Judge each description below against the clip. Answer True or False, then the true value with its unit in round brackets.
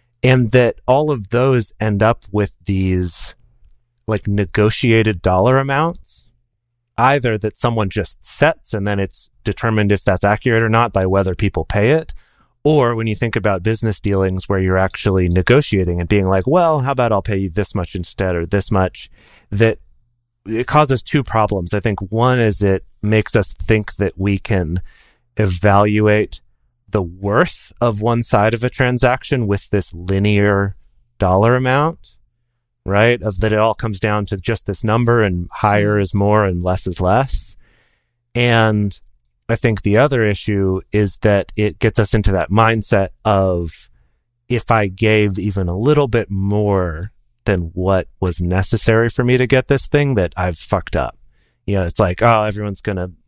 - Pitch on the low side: True (105 Hz)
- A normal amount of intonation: True (3.4 semitones)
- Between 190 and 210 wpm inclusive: False (170 wpm)